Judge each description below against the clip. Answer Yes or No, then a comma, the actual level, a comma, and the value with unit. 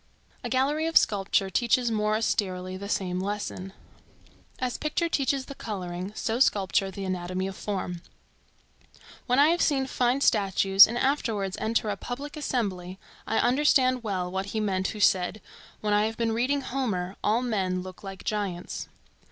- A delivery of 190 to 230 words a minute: No, average, 160 wpm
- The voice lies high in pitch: Yes, high, 210 Hz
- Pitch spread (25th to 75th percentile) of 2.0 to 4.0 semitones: No, average, 4.8 semitones